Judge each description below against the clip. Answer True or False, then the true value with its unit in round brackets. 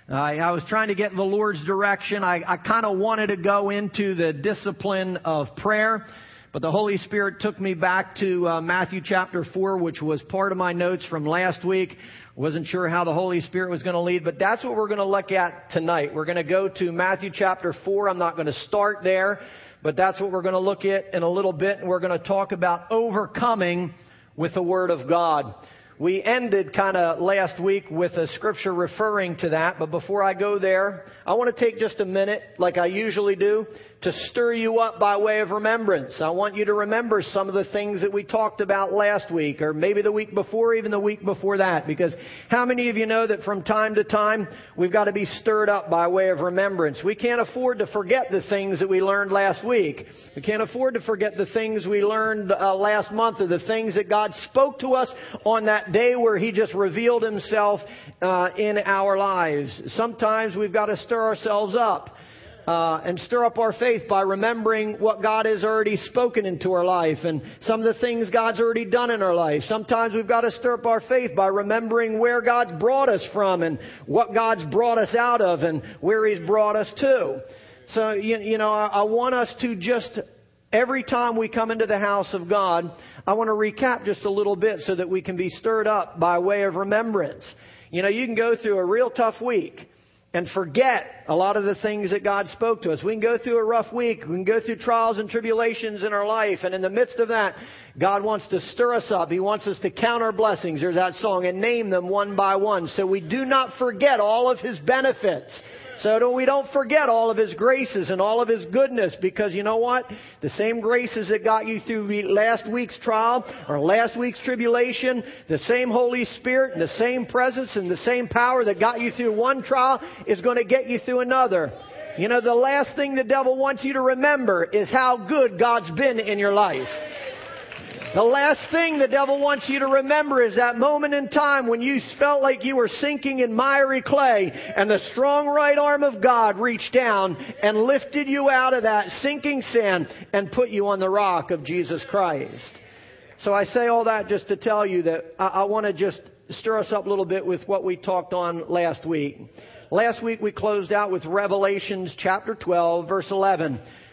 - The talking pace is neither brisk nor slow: False (220 wpm)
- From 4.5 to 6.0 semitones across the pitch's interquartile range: False (3.7 semitones)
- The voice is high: True (210 Hz)